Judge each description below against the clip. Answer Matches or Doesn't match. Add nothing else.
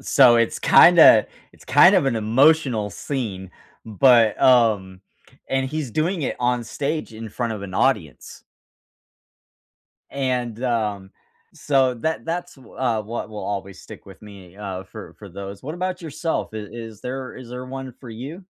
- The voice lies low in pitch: Matches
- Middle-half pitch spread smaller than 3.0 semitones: Doesn't match